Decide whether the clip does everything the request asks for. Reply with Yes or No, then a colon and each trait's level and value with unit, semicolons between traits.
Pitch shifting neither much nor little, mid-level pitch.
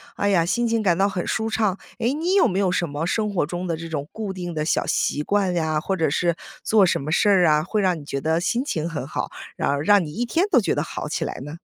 Yes: average, 4.7 semitones; medium, 180 Hz